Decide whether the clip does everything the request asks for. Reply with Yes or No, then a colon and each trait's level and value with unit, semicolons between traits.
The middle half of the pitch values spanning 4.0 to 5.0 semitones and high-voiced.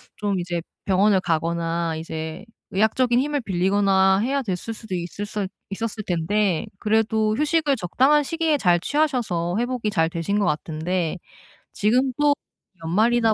No: wide, 5.5 semitones; high, 205 Hz